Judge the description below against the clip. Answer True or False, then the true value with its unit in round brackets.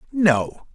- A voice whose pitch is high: False (170 Hz)